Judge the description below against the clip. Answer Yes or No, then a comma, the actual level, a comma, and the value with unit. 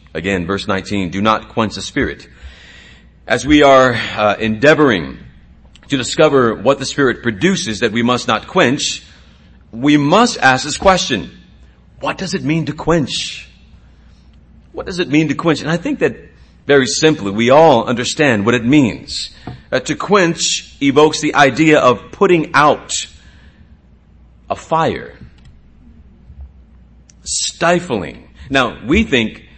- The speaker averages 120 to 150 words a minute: Yes, average, 140 wpm